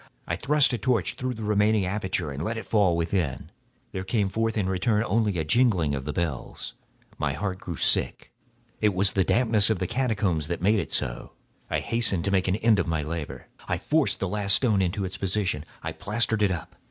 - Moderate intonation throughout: Yes, average, 4.0 semitones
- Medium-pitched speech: No, low, 100 Hz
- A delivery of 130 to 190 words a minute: No, average, 200 wpm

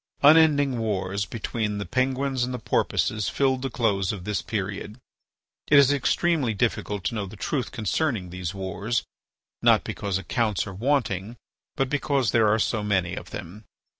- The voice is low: Yes, low, 110 Hz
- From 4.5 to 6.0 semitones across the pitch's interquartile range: Yes, average, 4.9 semitones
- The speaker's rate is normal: Yes, average, 165 wpm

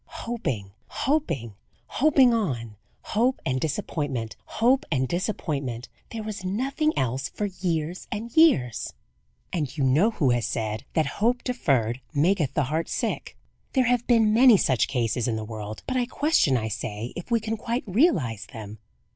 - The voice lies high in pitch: No, medium, 160 Hz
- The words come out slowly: No, average, 160 wpm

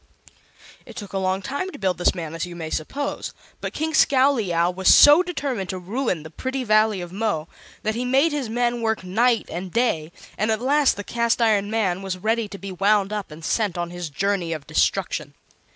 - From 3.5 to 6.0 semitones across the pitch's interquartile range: Yes, average, 5.0 semitones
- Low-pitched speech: No, high, 205 Hz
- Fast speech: Yes, fast, 210 wpm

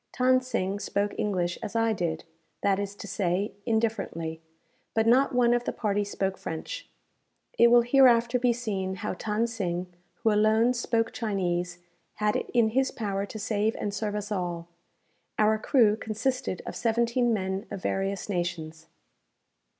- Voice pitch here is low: No, high, 210 Hz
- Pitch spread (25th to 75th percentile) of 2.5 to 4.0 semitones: Yes, average, 3.5 semitones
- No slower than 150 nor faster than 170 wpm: Yes, average, 160 wpm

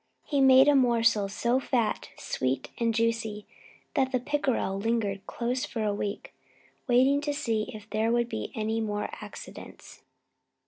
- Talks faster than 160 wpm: No, average, 150 wpm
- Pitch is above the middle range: Yes, high, 230 Hz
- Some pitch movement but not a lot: Yes, average, 3.2 semitones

